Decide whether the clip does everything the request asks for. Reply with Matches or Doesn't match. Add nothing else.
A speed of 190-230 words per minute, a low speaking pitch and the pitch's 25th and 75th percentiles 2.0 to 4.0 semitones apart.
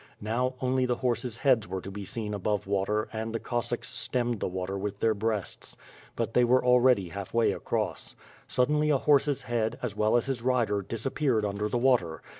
Matches